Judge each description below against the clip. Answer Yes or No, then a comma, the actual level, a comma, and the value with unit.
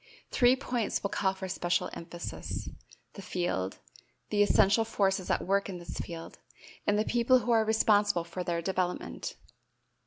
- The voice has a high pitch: Yes, high, 195 Hz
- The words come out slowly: No, average, 155 wpm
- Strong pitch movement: No, average, 3.6 semitones